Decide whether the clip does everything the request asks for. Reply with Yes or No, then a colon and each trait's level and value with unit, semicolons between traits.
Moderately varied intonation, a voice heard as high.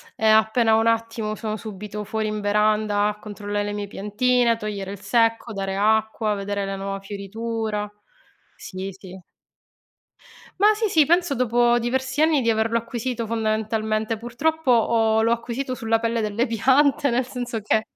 No: narrow, 2.3 semitones; high, 220 Hz